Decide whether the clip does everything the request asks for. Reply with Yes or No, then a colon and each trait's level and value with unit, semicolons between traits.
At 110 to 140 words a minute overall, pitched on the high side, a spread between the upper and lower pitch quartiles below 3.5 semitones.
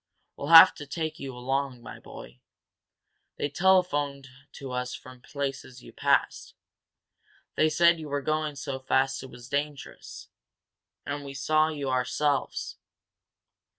No: slow, 135 wpm; medium, 140 Hz; narrow, 2.5 semitones